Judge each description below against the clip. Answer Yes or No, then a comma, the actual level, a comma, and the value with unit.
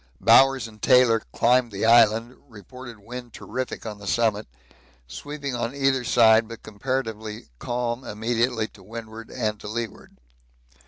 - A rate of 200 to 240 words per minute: No, average, 140 wpm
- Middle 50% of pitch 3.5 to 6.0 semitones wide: No, narrow, 2.4 semitones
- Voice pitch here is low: Yes, low, 115 Hz